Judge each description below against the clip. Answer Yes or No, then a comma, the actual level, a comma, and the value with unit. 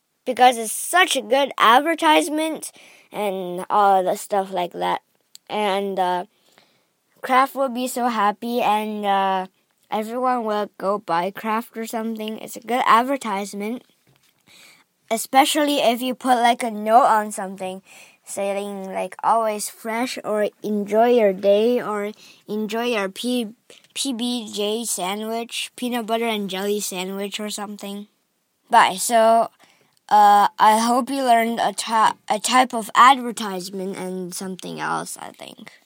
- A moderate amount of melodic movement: Yes, average, 3.3 semitones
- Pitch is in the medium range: No, high, 215 Hz